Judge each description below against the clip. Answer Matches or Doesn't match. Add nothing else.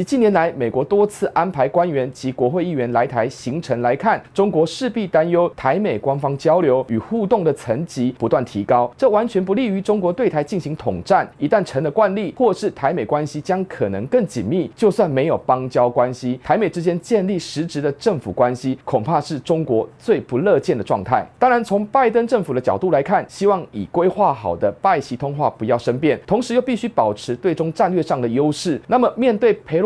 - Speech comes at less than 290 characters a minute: Doesn't match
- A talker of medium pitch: Matches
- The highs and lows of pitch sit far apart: Matches